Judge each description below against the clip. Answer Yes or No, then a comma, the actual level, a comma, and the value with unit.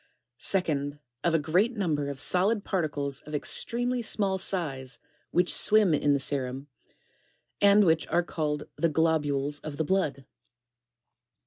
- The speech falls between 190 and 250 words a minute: No, average, 140 wpm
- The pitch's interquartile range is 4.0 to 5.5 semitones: Yes, average, 4.9 semitones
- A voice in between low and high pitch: Yes, medium, 160 Hz